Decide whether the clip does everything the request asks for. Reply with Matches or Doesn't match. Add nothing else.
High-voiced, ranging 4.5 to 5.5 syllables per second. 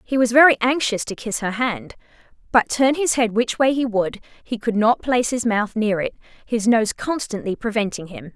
Matches